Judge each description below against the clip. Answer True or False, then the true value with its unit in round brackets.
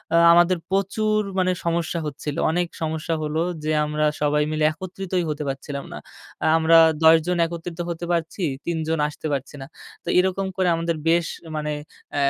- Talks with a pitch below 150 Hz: False (165 Hz)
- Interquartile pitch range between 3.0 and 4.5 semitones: False (2.6 semitones)